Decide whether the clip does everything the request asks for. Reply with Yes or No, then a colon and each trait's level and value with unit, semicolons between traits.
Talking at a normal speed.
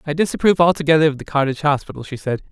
No: fast, 215 wpm